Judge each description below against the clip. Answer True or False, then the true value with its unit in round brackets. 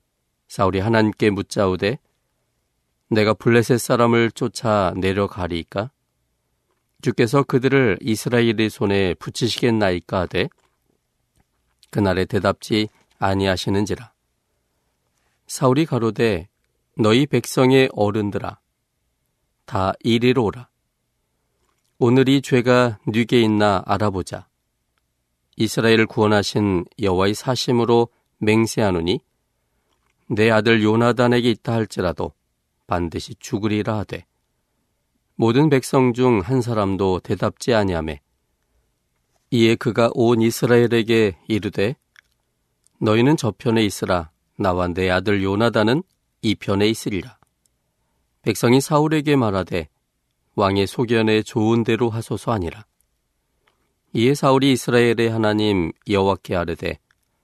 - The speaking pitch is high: False (110 Hz)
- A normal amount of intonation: True (4.2 semitones)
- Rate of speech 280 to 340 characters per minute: False (250 characters per minute)